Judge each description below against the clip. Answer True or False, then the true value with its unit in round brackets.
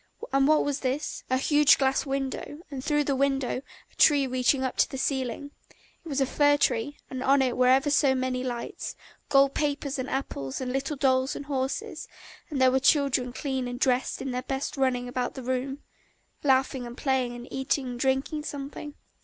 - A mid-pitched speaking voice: False (265 Hz)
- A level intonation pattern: True (1.6 semitones)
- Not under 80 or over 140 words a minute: False (195 wpm)